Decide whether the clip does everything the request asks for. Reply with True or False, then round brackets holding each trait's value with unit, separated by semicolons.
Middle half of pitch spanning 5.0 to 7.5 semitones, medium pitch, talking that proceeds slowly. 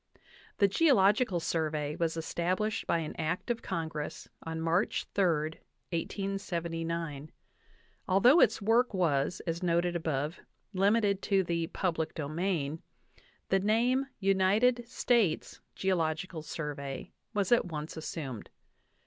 False (3.7 semitones; 175 Hz; 115 wpm)